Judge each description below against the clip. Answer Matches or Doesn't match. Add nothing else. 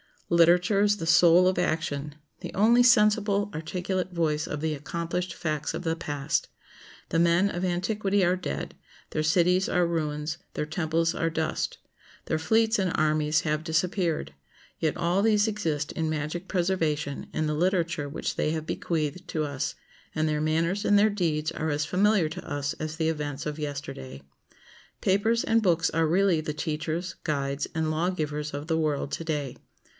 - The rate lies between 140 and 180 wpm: Matches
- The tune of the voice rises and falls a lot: Doesn't match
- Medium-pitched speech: Matches